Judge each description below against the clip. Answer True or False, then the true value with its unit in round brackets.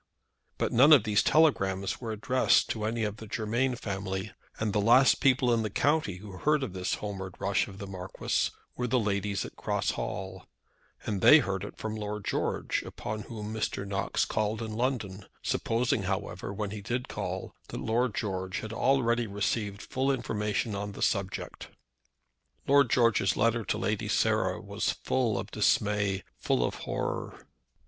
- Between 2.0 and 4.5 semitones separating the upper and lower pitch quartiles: True (3.0 semitones)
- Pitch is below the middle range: True (105 Hz)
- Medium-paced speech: True (170 wpm)